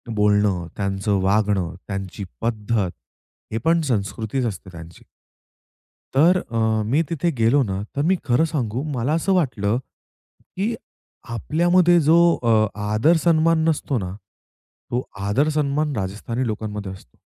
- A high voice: No, low, 115 Hz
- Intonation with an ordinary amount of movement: No, wide, 7.1 semitones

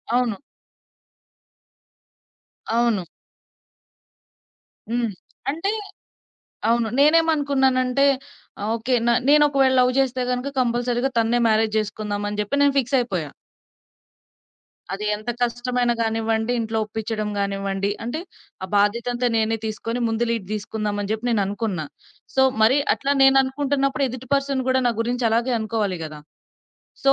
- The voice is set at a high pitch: Yes, high, 235 Hz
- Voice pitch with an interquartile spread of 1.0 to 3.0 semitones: No, average, 3.4 semitones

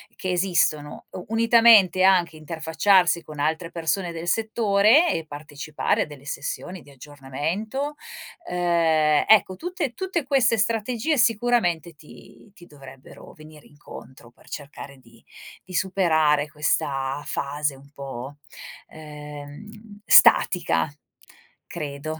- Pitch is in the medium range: Yes, medium, 165 Hz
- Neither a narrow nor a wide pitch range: No, wide, 5.9 semitones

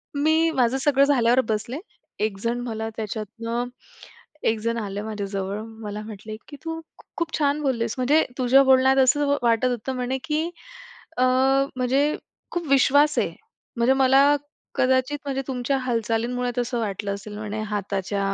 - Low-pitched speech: No, high, 245 Hz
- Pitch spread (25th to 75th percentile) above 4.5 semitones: No, average, 3.8 semitones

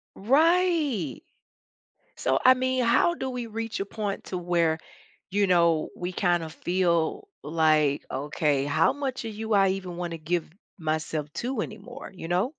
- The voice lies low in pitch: No, medium, 185 Hz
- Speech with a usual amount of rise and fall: No, wide, 6.7 semitones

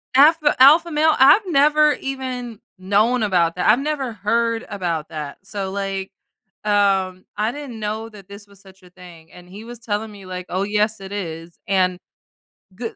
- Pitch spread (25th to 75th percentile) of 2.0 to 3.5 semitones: No, average, 4.7 semitones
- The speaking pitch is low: No, high, 205 Hz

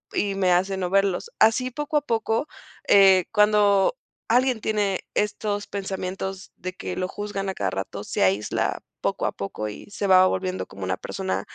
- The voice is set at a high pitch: Yes, high, 195 Hz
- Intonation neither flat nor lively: No, narrow, 2.2 semitones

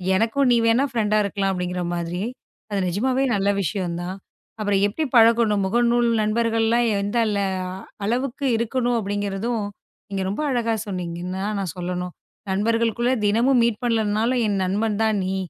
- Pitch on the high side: Yes, high, 215 Hz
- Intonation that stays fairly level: No, average, 3.3 semitones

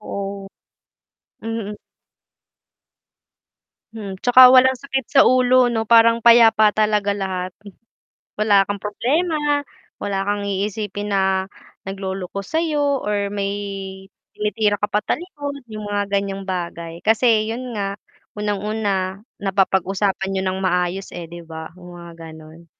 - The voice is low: No, high, 205 Hz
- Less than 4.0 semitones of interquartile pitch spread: Yes, average, 2.9 semitones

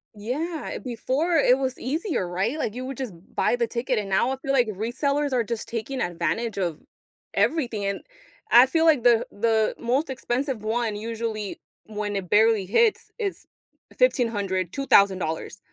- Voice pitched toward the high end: Yes, high, 235 Hz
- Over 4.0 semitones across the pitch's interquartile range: Yes, average, 4.4 semitones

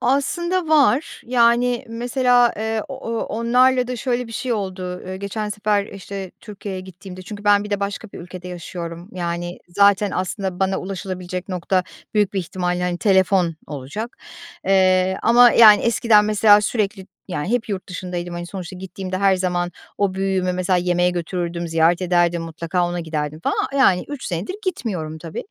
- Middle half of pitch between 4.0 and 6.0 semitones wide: No, average, 3.4 semitones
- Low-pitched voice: No, high, 190 Hz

